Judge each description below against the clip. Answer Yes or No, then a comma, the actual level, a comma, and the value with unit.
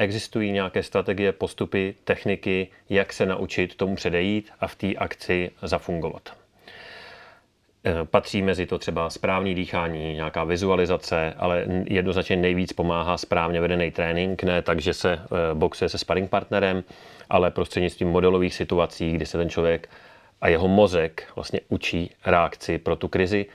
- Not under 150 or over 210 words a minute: No, average, 140 wpm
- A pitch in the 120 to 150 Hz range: No, very low, 90 Hz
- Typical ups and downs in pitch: No, narrow, 2.1 semitones